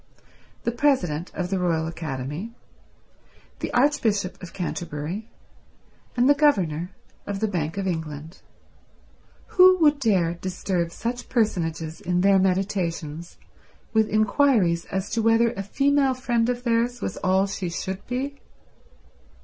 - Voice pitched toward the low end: No, high, 195 Hz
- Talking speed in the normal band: No, slow, 125 wpm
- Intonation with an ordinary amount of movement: No, wide, 5.8 semitones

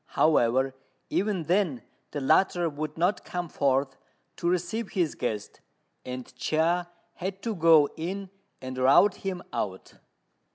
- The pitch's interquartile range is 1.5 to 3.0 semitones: No, average, 5.3 semitones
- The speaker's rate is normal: No, slow, 130 wpm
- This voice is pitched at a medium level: Yes, medium, 165 Hz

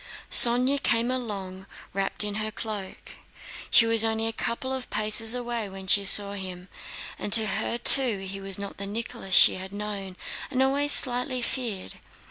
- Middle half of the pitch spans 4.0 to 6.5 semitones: No, average, 3.6 semitones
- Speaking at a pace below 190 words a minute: Yes, average, 170 wpm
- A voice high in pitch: Yes, high, 215 Hz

